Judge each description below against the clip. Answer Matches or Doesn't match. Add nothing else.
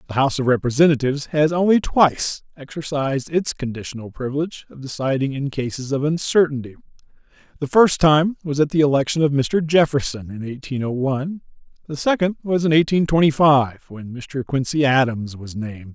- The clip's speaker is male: Matches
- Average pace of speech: Matches